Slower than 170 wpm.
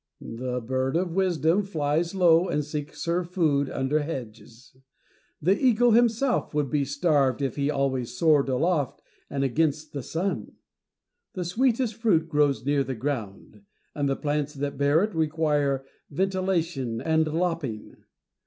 Yes: average, 145 wpm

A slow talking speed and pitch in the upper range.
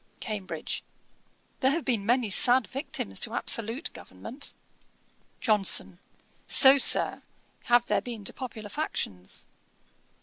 Yes: slow, 110 wpm; high, 240 Hz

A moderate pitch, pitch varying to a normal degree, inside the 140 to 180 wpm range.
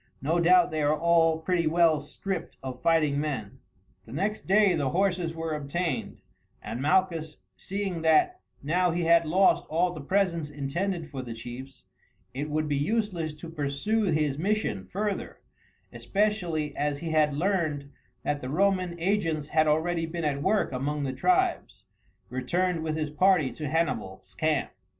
Yes: medium, 160 Hz; average, 3.8 semitones; average, 160 wpm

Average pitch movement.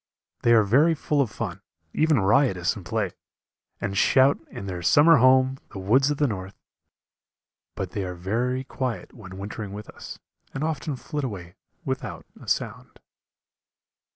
No: wide, 5.7 semitones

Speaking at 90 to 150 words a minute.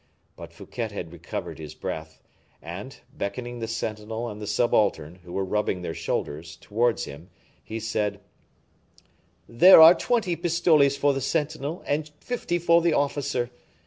Yes: average, 145 wpm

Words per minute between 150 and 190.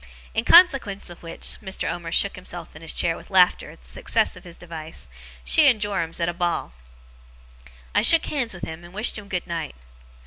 No: fast, 205 wpm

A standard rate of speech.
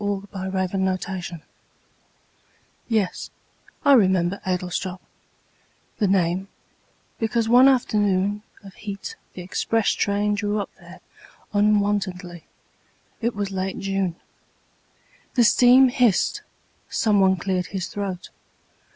No: slow, 100 wpm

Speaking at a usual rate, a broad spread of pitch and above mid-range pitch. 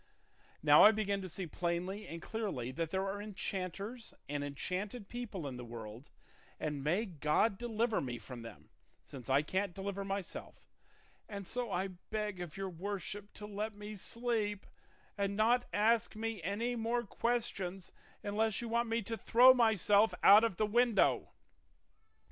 No: average, 160 wpm; average, 4.0 semitones; high, 200 Hz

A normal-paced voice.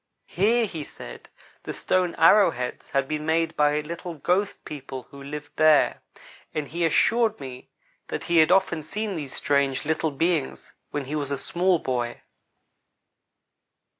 Yes: average, 155 wpm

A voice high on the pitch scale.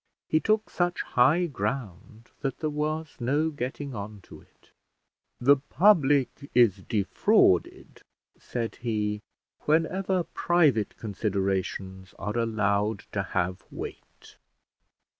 No: low, 120 Hz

